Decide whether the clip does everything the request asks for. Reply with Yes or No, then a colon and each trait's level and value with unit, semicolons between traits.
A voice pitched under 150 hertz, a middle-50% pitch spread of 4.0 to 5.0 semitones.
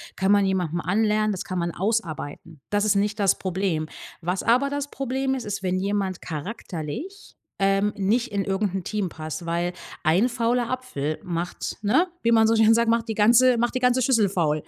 No: high, 205 Hz; average, 4.5 semitones